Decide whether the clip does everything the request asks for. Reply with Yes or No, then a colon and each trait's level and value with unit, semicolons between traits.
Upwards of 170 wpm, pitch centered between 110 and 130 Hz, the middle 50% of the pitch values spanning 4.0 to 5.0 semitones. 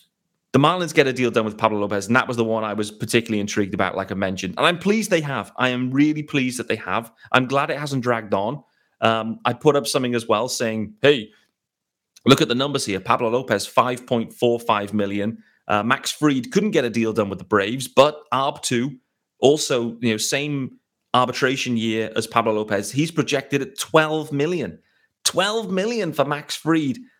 Yes: average, 200 wpm; low, 125 Hz; average, 4.5 semitones